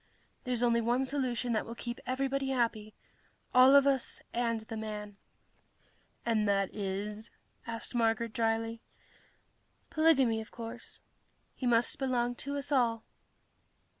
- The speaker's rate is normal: No, slow, 130 wpm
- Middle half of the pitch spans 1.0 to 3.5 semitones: Yes, narrow, 2.5 semitones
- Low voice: No, high, 235 Hz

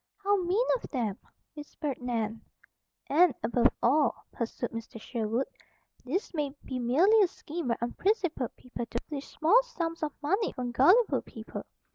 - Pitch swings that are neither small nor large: No, wide, 6.7 semitones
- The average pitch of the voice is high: Yes, very high, 285 Hz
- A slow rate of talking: No, average, 150 wpm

